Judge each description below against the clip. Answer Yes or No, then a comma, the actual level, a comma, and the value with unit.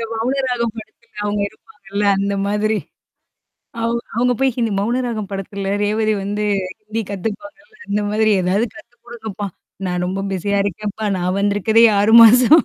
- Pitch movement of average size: No, narrow, 2.3 semitones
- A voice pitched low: No, high, 215 Hz